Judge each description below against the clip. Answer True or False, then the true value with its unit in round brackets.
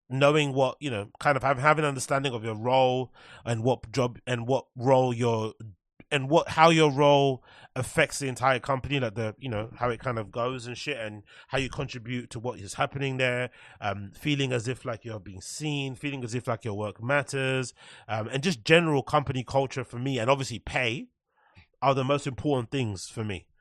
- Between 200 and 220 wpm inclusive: True (205 wpm)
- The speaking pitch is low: True (130 Hz)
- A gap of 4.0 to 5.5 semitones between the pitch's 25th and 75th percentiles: False (3.0 semitones)